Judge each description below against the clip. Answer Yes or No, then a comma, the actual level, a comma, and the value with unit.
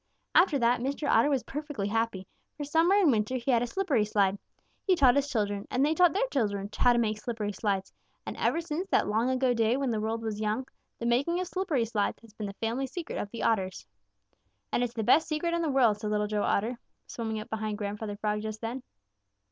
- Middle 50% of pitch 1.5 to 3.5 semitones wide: No, average, 4.9 semitones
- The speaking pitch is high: Yes, high, 235 Hz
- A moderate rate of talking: No, fast, 230 wpm